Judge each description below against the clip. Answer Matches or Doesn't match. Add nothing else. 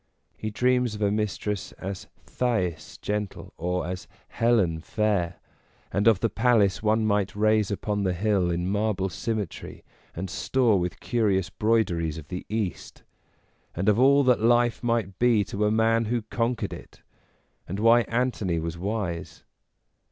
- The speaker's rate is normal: Matches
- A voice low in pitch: Matches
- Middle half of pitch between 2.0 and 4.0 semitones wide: Matches